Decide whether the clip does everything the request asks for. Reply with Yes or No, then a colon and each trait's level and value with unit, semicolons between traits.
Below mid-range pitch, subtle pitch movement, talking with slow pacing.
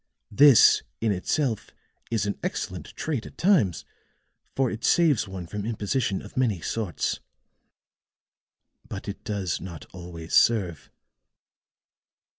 No: low, 105 Hz; average, 5.2 semitones; slow, 115 wpm